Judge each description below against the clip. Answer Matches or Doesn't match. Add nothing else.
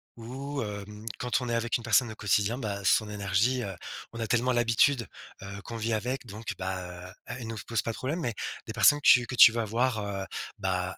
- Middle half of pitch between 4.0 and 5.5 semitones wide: Doesn't match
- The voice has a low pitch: Matches